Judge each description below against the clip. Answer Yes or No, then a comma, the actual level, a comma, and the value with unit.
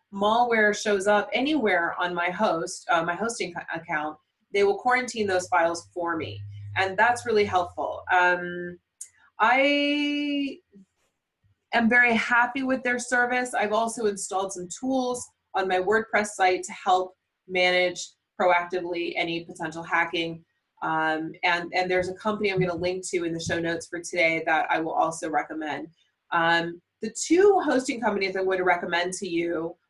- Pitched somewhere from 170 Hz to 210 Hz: Yes, medium, 185 Hz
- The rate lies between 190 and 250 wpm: No, average, 155 wpm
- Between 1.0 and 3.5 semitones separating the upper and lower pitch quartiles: No, average, 4.7 semitones